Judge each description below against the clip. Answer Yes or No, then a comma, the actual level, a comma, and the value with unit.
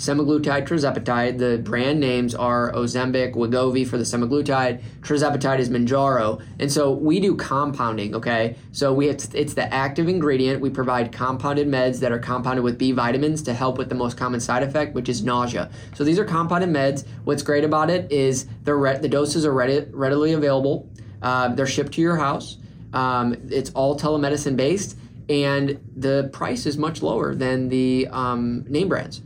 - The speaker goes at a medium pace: Yes, average, 175 wpm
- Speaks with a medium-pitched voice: No, low, 130 Hz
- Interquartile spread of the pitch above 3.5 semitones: No, average, 2.9 semitones